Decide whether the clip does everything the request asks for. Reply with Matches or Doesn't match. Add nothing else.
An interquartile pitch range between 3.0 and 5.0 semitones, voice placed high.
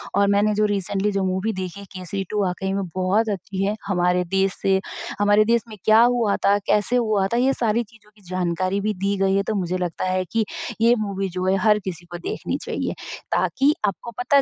Doesn't match